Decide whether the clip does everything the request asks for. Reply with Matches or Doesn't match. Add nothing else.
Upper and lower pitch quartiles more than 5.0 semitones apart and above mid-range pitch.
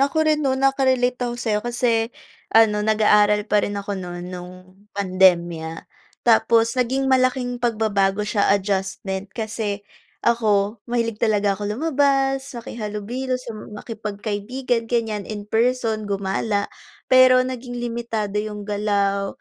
Doesn't match